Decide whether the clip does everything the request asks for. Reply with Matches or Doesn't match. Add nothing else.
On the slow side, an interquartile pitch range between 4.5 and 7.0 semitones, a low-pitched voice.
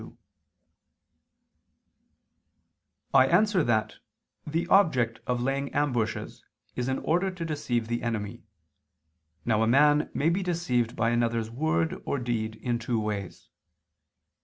Matches